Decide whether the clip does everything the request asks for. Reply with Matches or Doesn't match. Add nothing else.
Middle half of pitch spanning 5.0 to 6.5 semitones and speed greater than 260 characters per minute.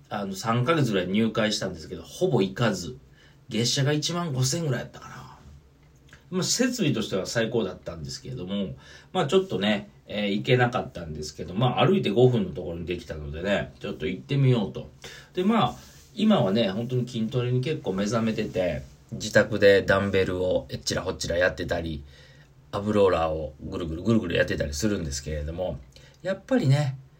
Doesn't match